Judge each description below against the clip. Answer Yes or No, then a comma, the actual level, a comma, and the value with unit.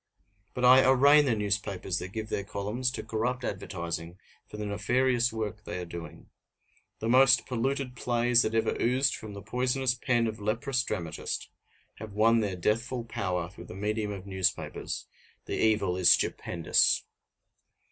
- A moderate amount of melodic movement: Yes, average, 3.8 semitones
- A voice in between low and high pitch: No, low, 110 Hz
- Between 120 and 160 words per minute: Yes, average, 155 wpm